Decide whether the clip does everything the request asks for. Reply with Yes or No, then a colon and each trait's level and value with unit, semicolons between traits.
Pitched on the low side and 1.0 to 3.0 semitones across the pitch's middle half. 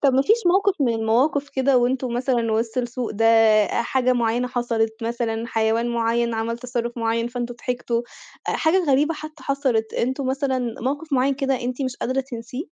No: high, 245 Hz; narrow, 2.6 semitones